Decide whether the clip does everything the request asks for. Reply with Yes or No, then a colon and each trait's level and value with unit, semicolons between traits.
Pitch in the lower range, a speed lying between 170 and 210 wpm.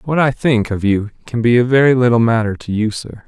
No: low, 120 Hz; fast, 255 wpm